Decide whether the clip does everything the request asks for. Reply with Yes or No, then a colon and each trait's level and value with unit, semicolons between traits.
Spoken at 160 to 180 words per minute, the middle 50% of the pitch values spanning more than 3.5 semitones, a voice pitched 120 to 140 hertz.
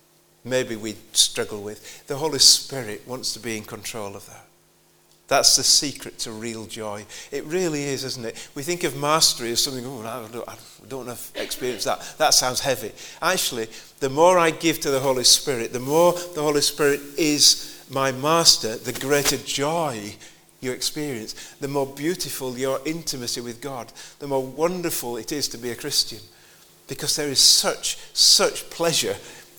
Yes: average, 175 wpm; average, 4.1 semitones; low, 135 Hz